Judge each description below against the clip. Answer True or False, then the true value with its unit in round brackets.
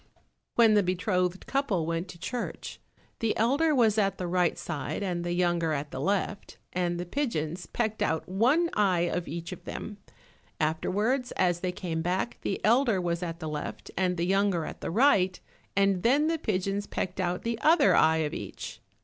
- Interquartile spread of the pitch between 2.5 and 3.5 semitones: False (4.2 semitones)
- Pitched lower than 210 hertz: True (185 Hz)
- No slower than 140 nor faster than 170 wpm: False (185 wpm)